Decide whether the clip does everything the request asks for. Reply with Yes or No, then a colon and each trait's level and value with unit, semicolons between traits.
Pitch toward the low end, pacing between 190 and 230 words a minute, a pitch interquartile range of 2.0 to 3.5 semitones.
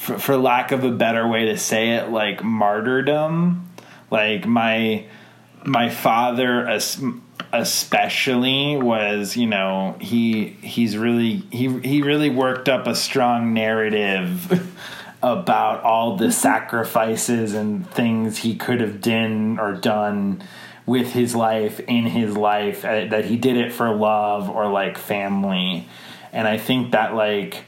No: low, 115 Hz; slow, 135 wpm; average, 2.7 semitones